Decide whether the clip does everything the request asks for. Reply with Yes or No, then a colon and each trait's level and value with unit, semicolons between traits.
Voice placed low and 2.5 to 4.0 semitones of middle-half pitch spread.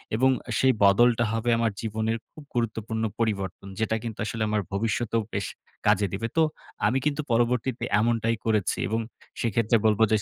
No: low, 115 Hz; narrow, 1.6 semitones